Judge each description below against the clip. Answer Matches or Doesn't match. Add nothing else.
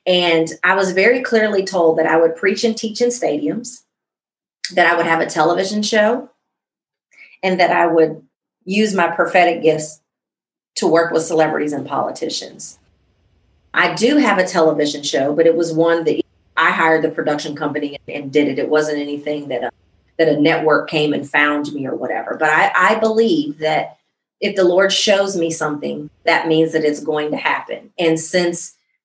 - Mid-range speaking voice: Matches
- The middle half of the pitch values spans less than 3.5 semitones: Doesn't match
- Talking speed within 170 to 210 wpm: Matches